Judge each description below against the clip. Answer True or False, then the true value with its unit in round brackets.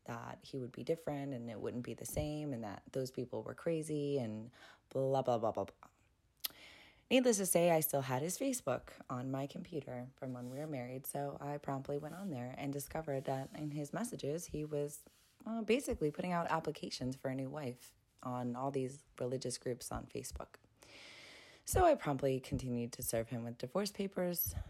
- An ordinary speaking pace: True (190 wpm)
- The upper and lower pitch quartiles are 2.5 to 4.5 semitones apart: True (3.6 semitones)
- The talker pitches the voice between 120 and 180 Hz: True (140 Hz)